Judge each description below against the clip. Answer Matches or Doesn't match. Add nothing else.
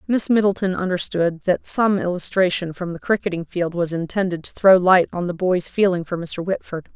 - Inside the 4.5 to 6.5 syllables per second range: Matches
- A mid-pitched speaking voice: Matches